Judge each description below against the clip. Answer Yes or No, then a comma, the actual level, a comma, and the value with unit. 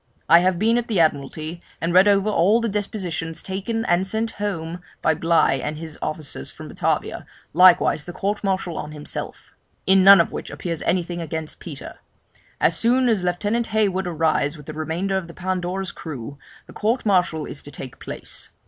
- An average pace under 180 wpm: No, average, 185 wpm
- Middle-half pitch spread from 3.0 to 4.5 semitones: Yes, average, 3.7 semitones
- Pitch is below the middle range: No, medium, 180 Hz